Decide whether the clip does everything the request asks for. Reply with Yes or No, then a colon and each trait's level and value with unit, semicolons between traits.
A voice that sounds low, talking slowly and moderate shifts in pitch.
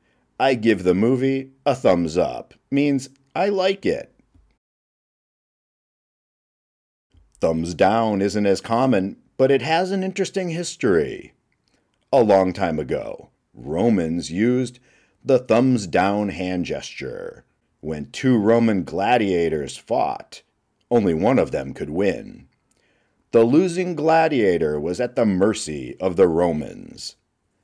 No: low, 115 Hz; slow, 115 wpm; wide, 6.8 semitones